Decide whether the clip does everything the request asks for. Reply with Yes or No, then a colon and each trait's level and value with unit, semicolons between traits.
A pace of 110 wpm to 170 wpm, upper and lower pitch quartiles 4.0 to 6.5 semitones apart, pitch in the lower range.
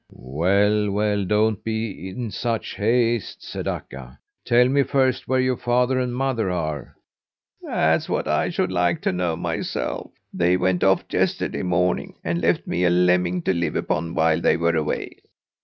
Yes: average, 165 wpm; average, 5.2 semitones; very low, 95 Hz